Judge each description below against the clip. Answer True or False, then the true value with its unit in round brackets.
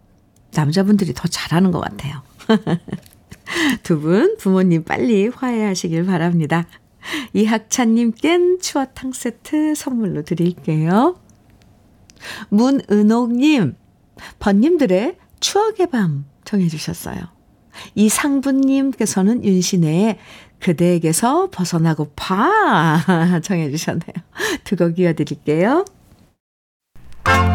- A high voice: True (195 Hz)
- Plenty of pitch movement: True (7.0 semitones)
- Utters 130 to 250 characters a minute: True (215 characters per minute)